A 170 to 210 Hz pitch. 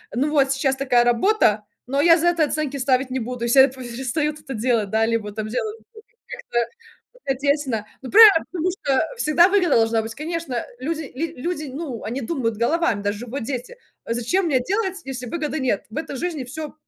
No: very high, 270 Hz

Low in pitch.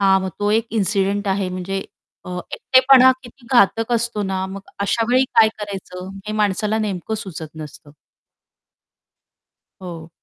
No: high, 200 Hz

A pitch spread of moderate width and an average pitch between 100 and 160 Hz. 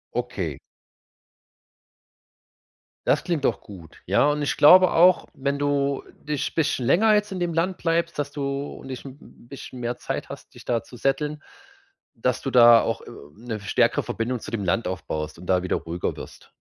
Yes: average, 4.8 semitones; medium, 140 Hz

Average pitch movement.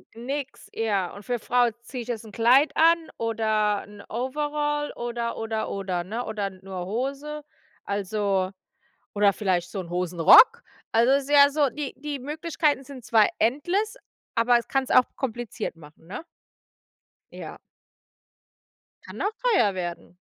No: wide, 5.7 semitones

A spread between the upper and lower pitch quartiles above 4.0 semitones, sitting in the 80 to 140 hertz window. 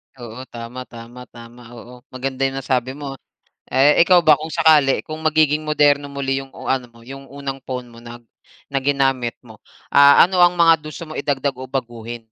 No: average, 3.0 semitones; low, 135 Hz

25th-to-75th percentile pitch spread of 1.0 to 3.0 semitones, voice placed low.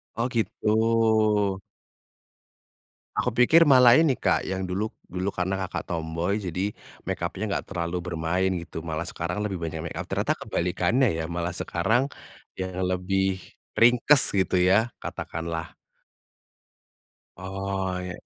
No: average, 3.8 semitones; very low, 95 Hz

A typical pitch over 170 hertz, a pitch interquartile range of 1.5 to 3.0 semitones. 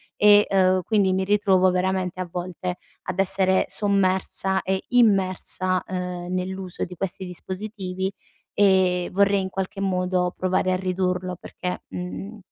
No: medium, 185 Hz; narrow, 1.1 semitones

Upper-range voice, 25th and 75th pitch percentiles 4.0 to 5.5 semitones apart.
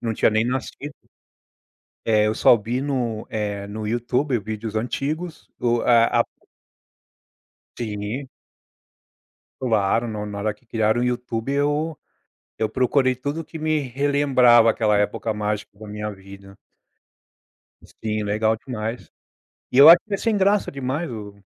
No: low, 115 Hz; average, 4.3 semitones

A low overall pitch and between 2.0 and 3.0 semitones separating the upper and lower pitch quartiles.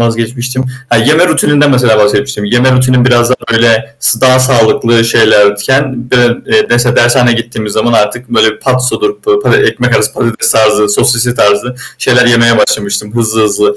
Yes: low, 120 Hz; narrow, 2.5 semitones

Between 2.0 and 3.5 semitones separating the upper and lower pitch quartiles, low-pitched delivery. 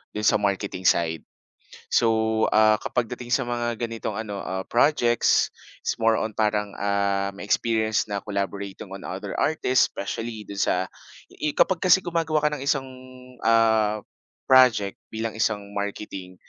Yes: average, 2.9 semitones; low, 110 Hz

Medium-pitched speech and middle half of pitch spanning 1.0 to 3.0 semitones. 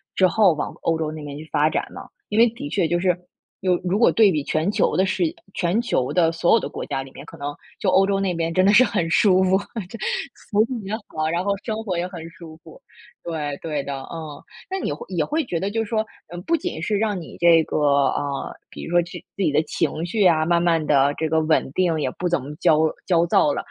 No: medium, 170 Hz; average, 3.8 semitones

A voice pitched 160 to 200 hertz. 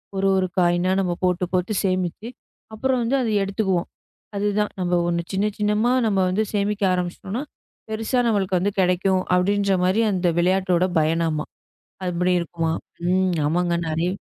Yes: medium, 185 Hz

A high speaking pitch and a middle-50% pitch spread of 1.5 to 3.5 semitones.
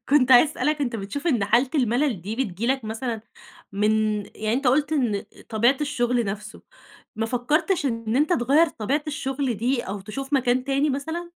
No: very high, 250 Hz; average, 4.3 semitones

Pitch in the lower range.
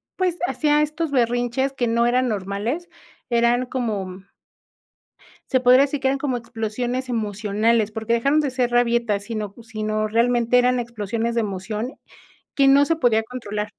No: high, 235 Hz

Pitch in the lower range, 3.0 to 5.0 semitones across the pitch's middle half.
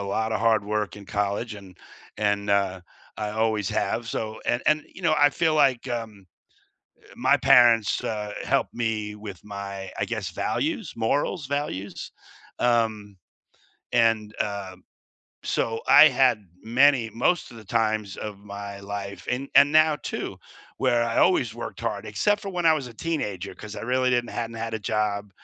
Yes: low, 110 Hz; average, 3.4 semitones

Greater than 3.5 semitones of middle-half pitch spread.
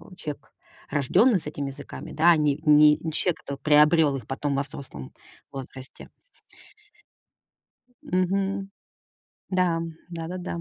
Yes: average, 4.0 semitones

